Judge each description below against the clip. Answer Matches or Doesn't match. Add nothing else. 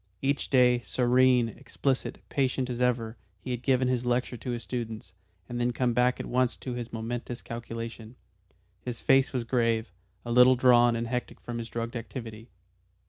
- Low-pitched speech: Matches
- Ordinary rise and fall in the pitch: Doesn't match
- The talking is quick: Doesn't match